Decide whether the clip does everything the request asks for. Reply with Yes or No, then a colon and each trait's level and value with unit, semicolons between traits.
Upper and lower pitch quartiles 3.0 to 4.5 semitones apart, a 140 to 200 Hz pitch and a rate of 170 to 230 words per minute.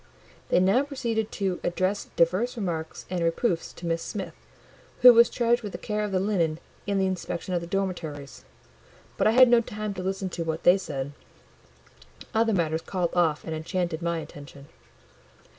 Yes: average, 4.0 semitones; medium, 185 Hz; average, 175 wpm